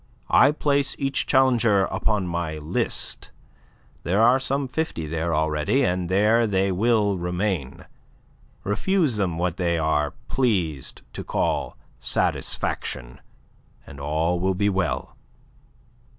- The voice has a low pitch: Yes, very low, 95 Hz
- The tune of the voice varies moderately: No, wide, 6.3 semitones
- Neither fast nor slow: No, slow, 120 wpm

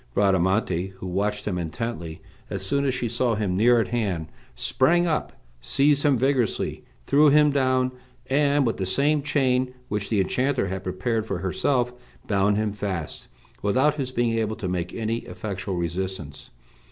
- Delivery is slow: No, average, 165 wpm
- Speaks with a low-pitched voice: Yes, low, 110 Hz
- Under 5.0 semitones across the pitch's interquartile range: No, wide, 5.4 semitones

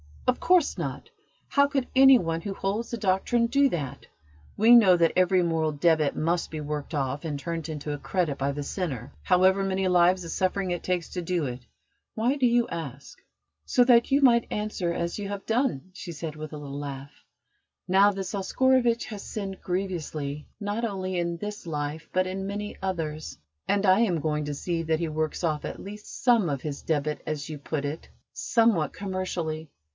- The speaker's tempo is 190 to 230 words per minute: Yes, average, 195 wpm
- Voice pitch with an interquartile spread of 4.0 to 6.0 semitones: Yes, average, 4.9 semitones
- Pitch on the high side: No, medium, 180 Hz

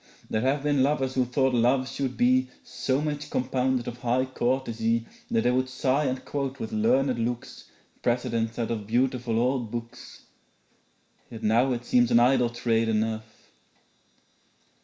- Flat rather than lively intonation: Yes, narrow, 2.1 semitones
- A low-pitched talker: Yes, low, 125 Hz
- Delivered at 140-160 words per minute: Yes, average, 155 wpm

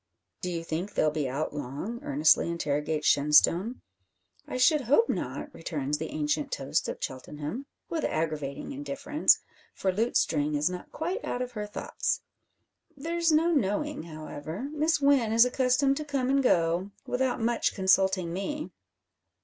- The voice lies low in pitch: No, high, 195 Hz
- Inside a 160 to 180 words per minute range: No, average, 150 wpm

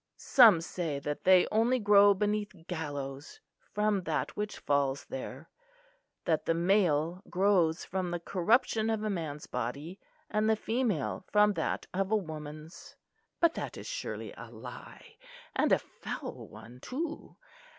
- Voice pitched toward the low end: No, medium, 185 Hz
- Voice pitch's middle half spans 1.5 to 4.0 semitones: No, wide, 5.6 semitones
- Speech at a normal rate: Yes, average, 145 wpm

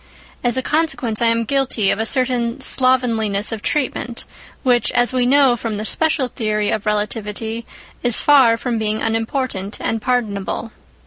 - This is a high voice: Yes, high, 235 Hz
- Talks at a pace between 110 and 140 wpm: No, average, 155 wpm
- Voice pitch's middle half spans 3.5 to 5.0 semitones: No, average, 2.8 semitones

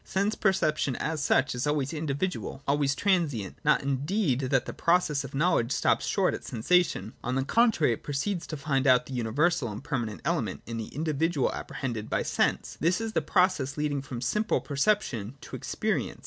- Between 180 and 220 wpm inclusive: Yes, average, 190 wpm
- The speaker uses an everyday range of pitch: Yes, average, 4.9 semitones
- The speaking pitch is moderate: Yes, medium, 145 Hz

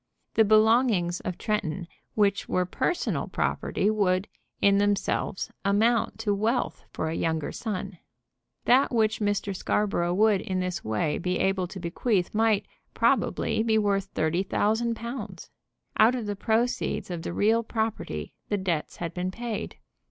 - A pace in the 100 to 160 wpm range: Yes, average, 150 wpm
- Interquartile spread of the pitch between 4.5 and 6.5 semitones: No, average, 3.3 semitones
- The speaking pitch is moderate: No, high, 205 Hz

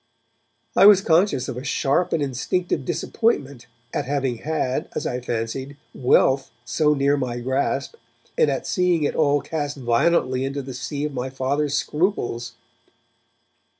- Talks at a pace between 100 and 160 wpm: Yes, average, 150 wpm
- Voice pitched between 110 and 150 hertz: Yes, medium, 140 Hz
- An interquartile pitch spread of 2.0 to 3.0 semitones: No, average, 3.6 semitones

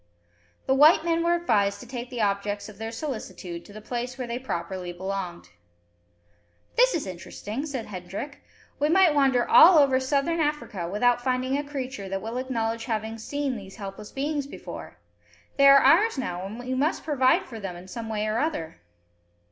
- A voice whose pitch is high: Yes, high, 245 Hz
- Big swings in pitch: Yes, wide, 5.7 semitones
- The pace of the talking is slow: No, average, 180 wpm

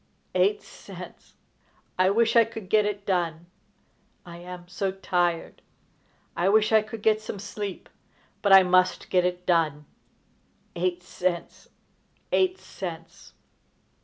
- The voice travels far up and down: No, average, 3.2 semitones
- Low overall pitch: No, medium, 185 Hz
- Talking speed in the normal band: No, slow, 130 wpm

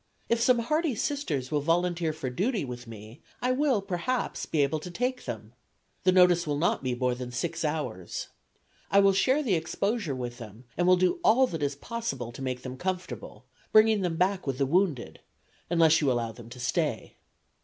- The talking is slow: No, average, 195 wpm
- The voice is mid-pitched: Yes, medium, 165 Hz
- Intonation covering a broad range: Yes, wide, 7.6 semitones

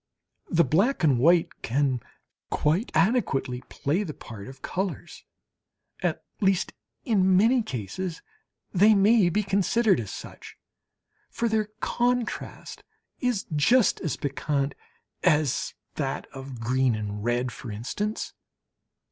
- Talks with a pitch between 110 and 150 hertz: No, medium, 165 Hz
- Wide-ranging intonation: Yes, wide, 8.0 semitones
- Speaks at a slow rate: Yes, slow, 120 wpm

